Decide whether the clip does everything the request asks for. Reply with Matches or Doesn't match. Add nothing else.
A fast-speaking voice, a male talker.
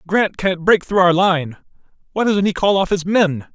Matches